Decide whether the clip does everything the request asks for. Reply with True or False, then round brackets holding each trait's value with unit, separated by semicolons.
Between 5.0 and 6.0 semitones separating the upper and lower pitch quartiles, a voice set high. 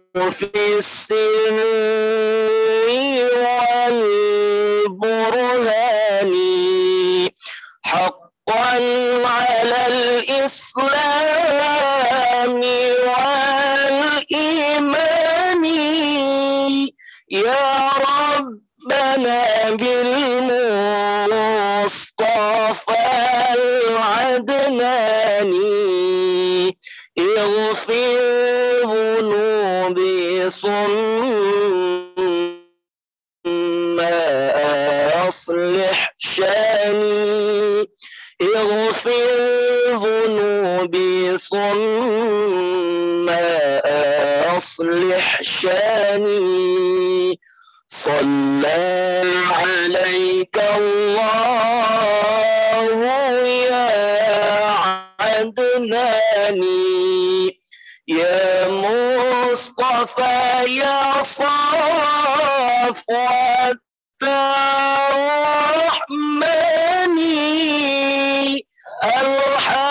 True (5.4 semitones; 245 Hz)